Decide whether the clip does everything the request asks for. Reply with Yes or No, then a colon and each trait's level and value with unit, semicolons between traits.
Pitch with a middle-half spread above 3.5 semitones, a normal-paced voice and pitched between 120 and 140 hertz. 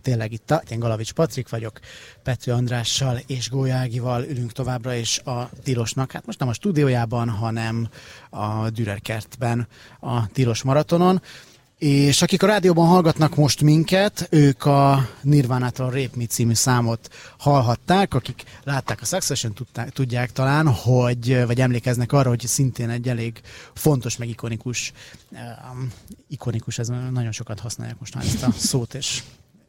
No: average, 2.8 semitones; average, 145 wpm; low, 125 Hz